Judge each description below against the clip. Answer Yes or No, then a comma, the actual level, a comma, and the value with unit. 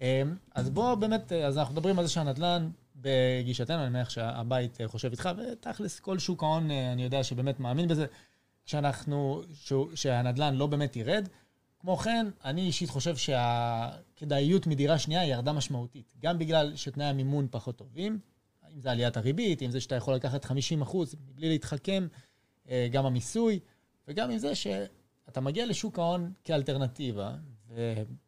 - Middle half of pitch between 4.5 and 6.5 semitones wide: Yes, average, 4.8 semitones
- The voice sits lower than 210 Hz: Yes, medium, 140 Hz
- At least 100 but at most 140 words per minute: No, fast, 150 wpm